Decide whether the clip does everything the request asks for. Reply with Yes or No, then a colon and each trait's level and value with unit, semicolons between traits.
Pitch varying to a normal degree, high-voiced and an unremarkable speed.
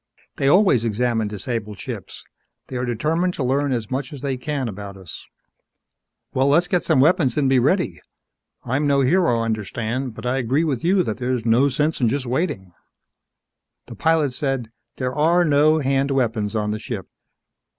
No: average, 4.3 semitones; low, 130 Hz; average, 175 wpm